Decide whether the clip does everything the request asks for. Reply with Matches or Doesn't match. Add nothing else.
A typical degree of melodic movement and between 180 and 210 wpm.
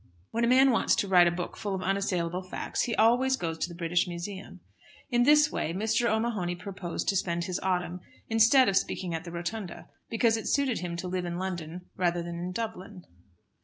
Matches